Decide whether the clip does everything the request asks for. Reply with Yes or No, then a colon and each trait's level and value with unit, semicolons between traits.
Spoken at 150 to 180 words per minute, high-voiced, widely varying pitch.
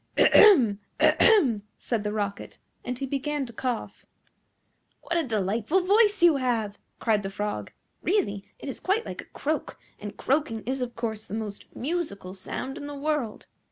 Yes: average, 165 wpm; very high, 250 Hz; wide, 6.4 semitones